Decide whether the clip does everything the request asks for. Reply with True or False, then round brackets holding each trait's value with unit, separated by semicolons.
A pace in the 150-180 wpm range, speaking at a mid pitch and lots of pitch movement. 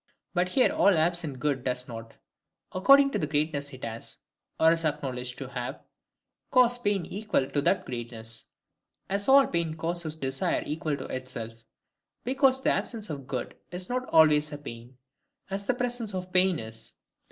True (165 wpm; 155 Hz; 7.3 semitones)